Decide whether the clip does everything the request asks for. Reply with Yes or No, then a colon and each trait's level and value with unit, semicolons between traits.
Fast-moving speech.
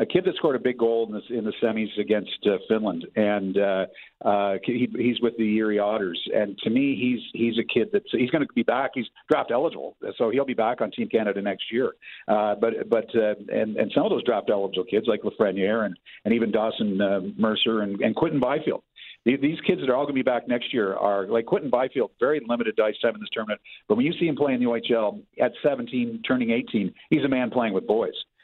Yes: fast, 245 wpm